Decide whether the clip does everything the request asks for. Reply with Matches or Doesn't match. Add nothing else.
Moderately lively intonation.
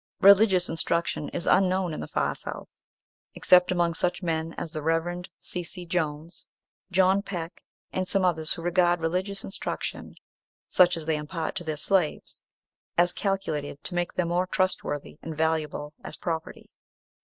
Doesn't match